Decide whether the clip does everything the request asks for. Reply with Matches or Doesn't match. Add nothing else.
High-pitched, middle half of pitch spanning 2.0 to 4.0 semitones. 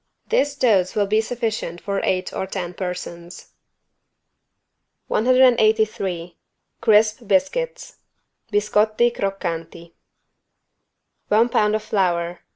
Matches